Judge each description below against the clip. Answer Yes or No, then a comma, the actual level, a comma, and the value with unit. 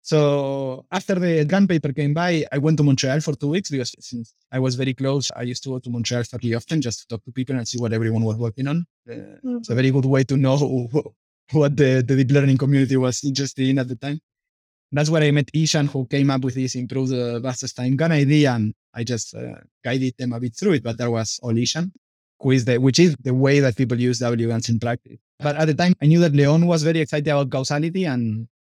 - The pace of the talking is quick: Yes, fast, 245 wpm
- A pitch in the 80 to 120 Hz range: No, low, 135 Hz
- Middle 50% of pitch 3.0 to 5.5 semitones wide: Yes, average, 3.3 semitones